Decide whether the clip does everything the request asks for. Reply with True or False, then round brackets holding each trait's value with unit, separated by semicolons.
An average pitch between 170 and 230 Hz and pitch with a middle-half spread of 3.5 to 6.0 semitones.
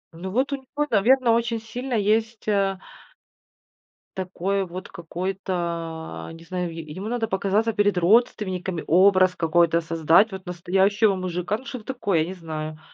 True (190 Hz; 4.2 semitones)